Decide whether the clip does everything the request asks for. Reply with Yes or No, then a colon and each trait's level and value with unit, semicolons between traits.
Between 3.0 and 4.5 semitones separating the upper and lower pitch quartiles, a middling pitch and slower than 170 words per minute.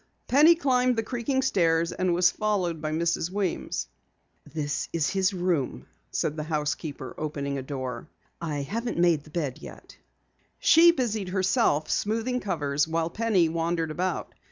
No: wide, 5.6 semitones; medium, 170 Hz; average, 150 wpm